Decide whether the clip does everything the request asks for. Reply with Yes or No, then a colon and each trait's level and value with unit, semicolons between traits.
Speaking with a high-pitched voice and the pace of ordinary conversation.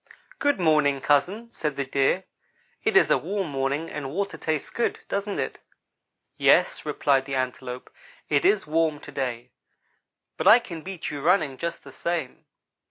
No: medium, 150 Hz; average, 165 wpm